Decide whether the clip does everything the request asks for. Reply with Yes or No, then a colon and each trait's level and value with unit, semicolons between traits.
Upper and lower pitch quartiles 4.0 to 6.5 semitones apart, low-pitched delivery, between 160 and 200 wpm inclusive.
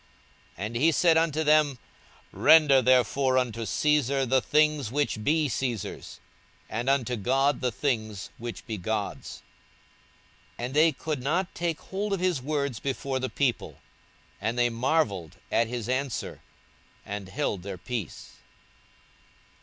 No: average, 4.5 semitones; low, 130 Hz; average, 140 wpm